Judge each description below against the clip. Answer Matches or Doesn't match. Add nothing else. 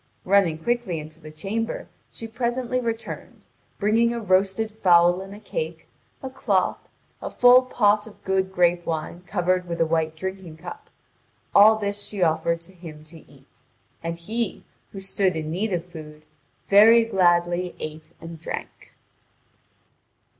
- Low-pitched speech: Doesn't match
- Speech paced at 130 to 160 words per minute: Matches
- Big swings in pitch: Doesn't match